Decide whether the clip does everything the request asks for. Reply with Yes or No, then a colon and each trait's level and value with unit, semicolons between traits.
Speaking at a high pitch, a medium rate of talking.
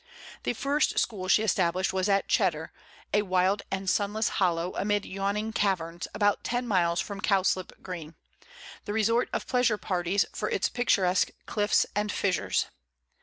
Yes: high, 195 Hz; average, 150 wpm